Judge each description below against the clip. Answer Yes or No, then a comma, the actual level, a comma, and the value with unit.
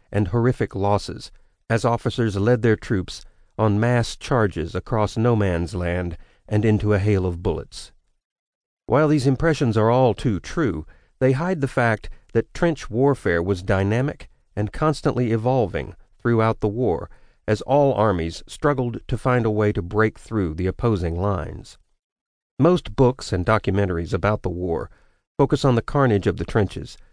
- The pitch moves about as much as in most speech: Yes, average, 4.3 semitones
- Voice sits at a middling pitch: No, low, 110 Hz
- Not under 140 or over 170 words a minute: Yes, average, 155 wpm